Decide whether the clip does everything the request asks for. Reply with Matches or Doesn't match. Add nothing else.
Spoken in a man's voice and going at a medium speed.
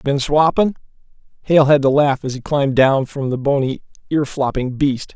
Matches